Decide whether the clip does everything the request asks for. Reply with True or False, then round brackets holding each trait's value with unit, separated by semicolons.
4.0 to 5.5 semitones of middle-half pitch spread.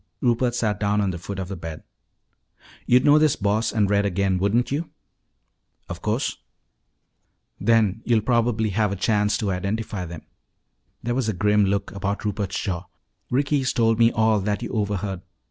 False (2.8 semitones)